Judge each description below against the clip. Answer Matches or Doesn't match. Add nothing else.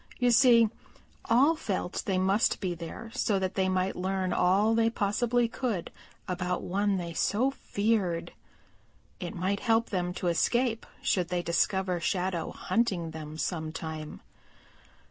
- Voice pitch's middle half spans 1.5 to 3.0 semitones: Doesn't match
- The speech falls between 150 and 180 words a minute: Doesn't match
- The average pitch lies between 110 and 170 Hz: Doesn't match